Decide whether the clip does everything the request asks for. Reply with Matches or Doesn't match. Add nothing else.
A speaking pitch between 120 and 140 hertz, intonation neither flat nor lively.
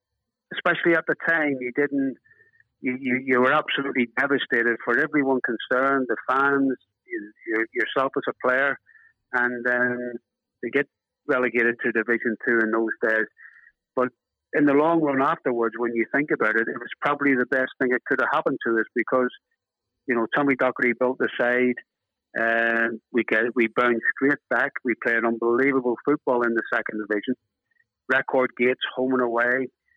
Matches